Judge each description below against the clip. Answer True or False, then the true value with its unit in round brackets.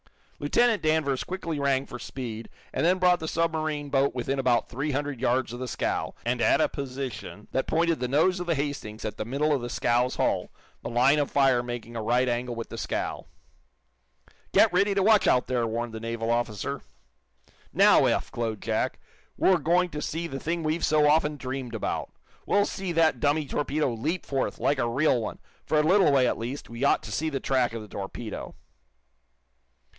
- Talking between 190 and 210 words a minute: True (200 wpm)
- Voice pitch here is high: False (135 Hz)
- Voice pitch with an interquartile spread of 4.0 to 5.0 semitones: True (4.6 semitones)